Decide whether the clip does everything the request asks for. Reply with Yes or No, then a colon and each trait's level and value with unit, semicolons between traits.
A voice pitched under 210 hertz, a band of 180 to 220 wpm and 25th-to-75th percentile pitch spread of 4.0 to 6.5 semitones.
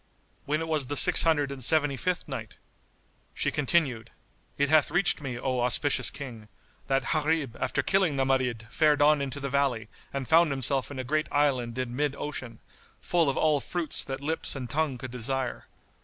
No: medium, 140 Hz; average, 185 wpm; average, 3.0 semitones